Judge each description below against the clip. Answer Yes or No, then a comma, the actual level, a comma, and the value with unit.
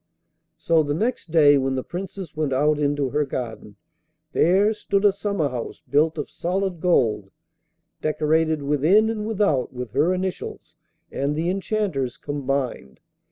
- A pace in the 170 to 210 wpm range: No, average, 145 wpm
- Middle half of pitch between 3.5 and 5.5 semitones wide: Yes, average, 5.2 semitones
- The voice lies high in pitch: No, medium, 155 Hz